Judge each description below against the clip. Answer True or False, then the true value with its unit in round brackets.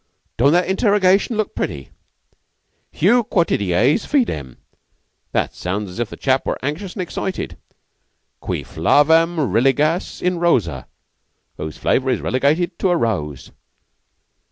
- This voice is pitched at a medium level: True (150 Hz)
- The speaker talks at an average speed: False (125 wpm)